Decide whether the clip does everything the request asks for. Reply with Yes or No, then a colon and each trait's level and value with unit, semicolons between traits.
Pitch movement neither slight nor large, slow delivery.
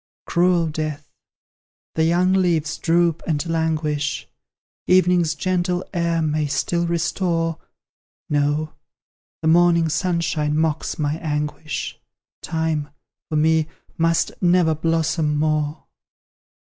No: narrow, 1.9 semitones; slow, 100 wpm